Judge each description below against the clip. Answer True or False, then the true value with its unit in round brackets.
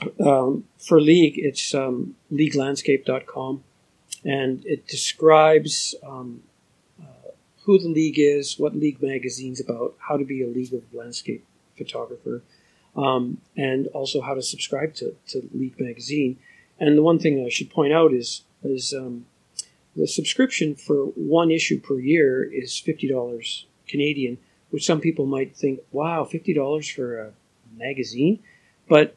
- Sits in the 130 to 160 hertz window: True (140 Hz)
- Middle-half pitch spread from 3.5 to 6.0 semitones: False (3.0 semitones)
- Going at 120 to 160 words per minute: True (145 wpm)